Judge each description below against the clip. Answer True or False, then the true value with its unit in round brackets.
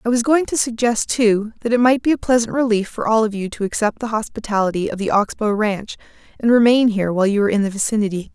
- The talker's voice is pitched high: True (220 Hz)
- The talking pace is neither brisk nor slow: False (250 wpm)